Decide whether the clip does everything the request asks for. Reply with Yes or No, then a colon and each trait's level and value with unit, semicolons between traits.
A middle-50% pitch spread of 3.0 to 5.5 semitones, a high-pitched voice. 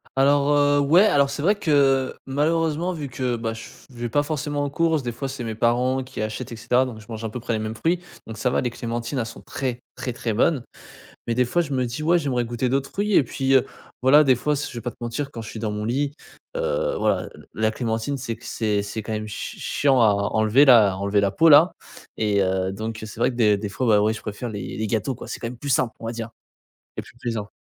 No: average, 4.1 semitones; low, 120 Hz